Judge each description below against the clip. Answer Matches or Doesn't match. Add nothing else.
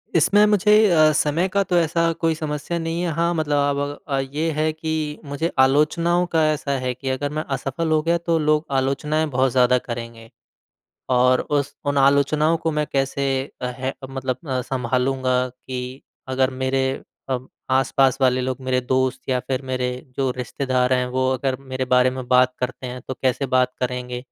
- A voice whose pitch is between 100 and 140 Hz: Matches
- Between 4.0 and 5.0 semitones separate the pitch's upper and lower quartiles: Doesn't match